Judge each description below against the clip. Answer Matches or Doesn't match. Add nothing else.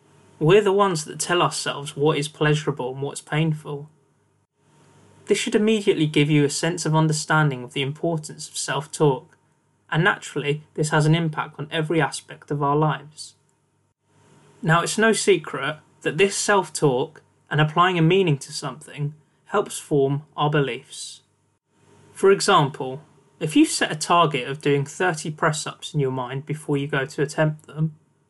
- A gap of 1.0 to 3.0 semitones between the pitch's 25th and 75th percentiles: Matches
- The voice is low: Doesn't match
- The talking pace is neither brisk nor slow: Matches